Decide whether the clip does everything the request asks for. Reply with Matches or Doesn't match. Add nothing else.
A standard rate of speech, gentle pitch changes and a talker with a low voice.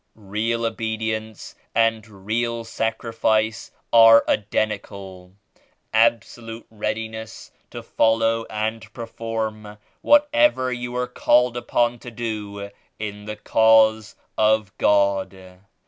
Doesn't match